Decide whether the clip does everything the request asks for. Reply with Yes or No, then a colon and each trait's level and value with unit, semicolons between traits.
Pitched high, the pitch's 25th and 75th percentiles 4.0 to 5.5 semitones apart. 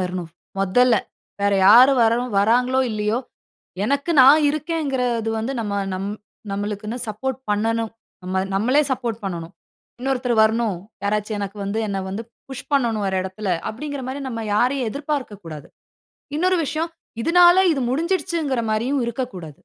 Yes: high, 235 Hz; average, 4.7 semitones